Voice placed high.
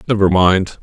No: very low, 95 Hz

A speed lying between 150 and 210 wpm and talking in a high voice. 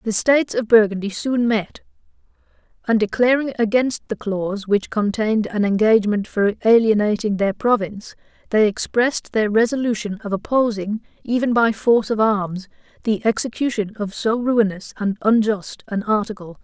No: average, 140 wpm; high, 215 Hz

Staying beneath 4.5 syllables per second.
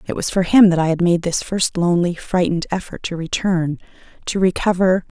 No: 5.6 syllables/s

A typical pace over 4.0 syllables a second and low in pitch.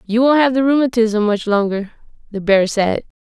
No: 5.1 syllables/s; high, 225 Hz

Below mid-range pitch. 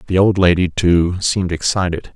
Yes: very low, 90 Hz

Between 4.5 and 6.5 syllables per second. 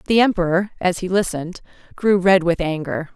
Yes: 5.5 syllables/s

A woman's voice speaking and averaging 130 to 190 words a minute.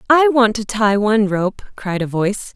No: female; fast, 210 wpm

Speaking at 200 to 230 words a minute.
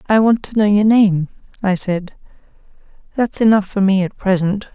No: average, 175 wpm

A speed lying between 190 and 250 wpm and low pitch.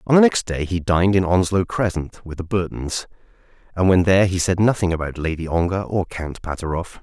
Yes: fast, 205 wpm; very low, 90 Hz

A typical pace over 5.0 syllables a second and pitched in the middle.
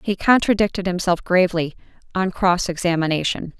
Yes: 5.5 syllables/s; medium, 180 Hz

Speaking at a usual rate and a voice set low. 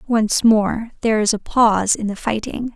No: average, 195 wpm; high, 220 Hz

